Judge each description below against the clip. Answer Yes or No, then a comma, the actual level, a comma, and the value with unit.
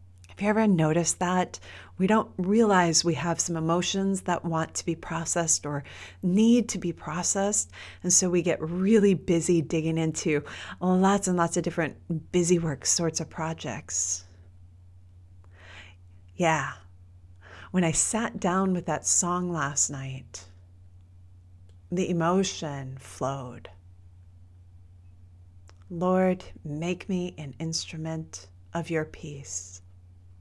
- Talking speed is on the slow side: Yes, slow, 120 wpm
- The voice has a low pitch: No, medium, 160 Hz